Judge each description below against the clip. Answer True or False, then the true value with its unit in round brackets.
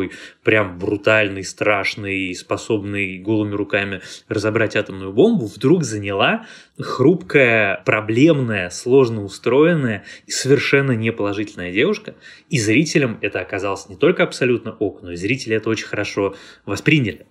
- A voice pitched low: True (110 Hz)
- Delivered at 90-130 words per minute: True (120 wpm)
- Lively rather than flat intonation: False (3.8 semitones)